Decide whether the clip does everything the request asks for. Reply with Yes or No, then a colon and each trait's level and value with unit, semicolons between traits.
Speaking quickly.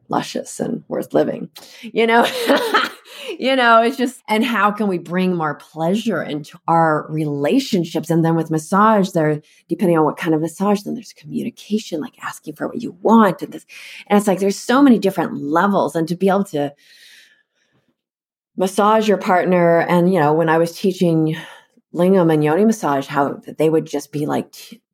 No: average, 185 wpm